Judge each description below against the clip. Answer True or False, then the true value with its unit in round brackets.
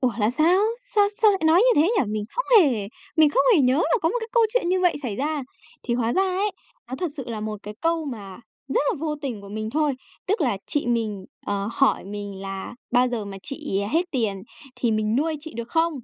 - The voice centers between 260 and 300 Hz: True (265 Hz)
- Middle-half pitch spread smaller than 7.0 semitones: False (7.4 semitones)